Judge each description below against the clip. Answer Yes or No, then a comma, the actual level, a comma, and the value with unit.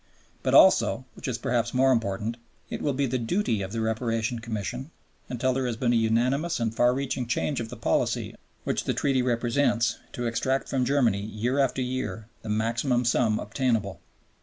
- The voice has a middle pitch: No, low, 120 Hz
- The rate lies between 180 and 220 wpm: Yes, average, 185 wpm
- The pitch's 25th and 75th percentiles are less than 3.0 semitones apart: Yes, narrow, 2.4 semitones